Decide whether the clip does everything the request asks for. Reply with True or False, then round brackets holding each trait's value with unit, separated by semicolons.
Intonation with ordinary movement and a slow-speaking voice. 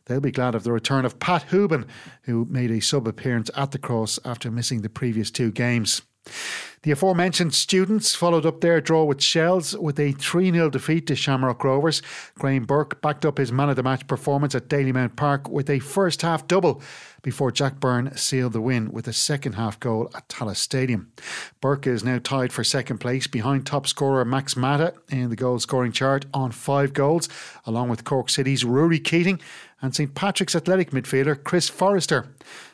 False (3.9 semitones; 185 wpm)